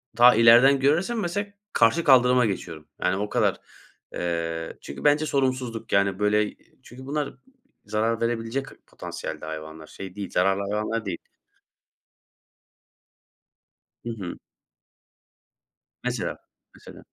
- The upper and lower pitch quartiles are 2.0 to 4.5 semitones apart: No, wide, 5.4 semitones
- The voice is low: Yes, low, 115 Hz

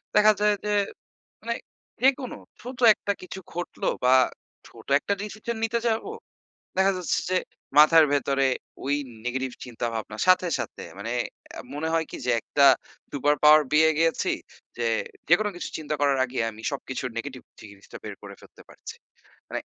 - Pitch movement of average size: No, wide, 7.4 semitones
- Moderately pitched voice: Yes, medium, 155 Hz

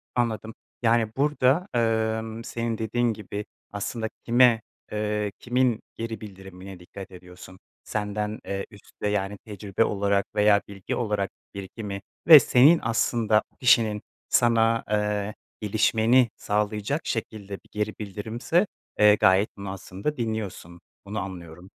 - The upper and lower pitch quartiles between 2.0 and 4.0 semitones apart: Yes, narrow, 2.4 semitones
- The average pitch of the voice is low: Yes, low, 105 Hz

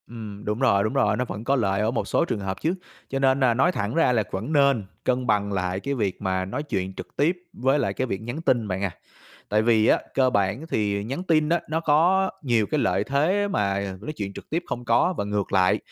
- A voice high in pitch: No, low, 120 Hz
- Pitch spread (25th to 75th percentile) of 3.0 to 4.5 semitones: No, wide, 5.6 semitones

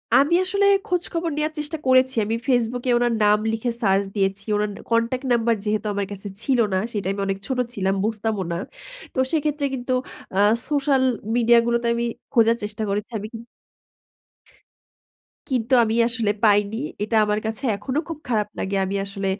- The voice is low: No, high, 230 Hz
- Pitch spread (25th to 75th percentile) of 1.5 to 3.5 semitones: No, average, 3.9 semitones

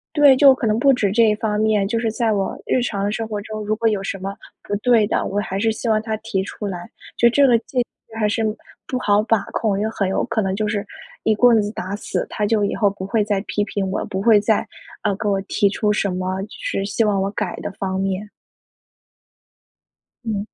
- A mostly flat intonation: Yes, narrow, 2.1 semitones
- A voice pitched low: No, high, 210 Hz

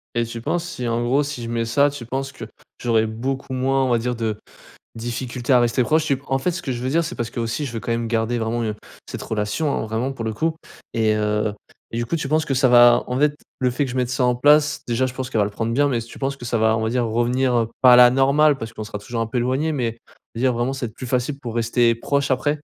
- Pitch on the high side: No, low, 125 Hz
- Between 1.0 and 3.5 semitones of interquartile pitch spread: Yes, narrow, 2.6 semitones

